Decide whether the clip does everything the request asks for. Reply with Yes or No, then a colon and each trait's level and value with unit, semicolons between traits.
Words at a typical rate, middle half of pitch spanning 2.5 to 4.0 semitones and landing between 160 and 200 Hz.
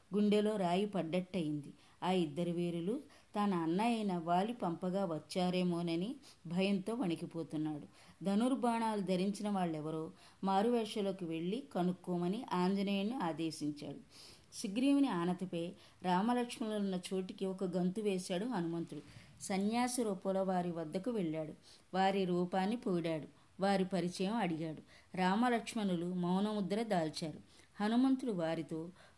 Yes: average, 95 wpm; average, 3.4 semitones; medium, 185 Hz